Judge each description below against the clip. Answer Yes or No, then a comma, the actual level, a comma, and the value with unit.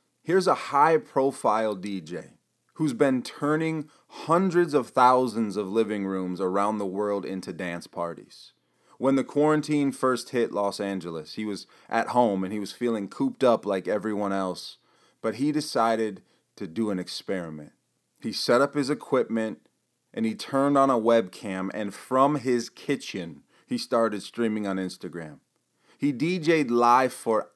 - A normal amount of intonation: No, wide, 5.7 semitones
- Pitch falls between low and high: No, low, 115 Hz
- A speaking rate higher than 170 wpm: No, average, 155 wpm